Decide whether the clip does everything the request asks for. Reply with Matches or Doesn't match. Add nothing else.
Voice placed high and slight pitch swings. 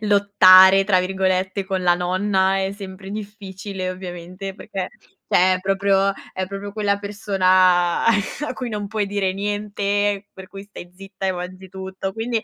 Matches